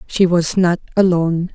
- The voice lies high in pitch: No, medium, 175 Hz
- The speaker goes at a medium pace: Yes, average, 155 wpm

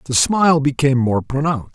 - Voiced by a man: Yes, male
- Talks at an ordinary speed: Yes, average, 170 wpm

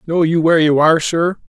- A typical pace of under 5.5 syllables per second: No, 6.3 syllables/s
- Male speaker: Yes, male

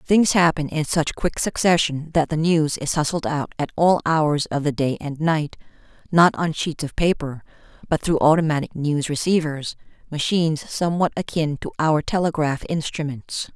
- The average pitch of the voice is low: No, medium, 155 Hz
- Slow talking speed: No, average, 165 wpm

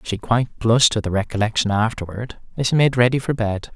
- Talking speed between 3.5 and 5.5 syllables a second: No, 6.0 syllables/s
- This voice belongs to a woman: No, male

